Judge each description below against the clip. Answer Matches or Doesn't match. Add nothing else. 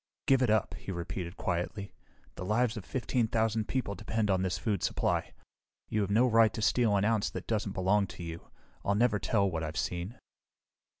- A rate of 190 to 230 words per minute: Matches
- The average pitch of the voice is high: Doesn't match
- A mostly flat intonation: Doesn't match